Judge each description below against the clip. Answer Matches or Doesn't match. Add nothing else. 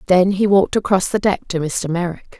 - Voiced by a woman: Matches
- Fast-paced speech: Matches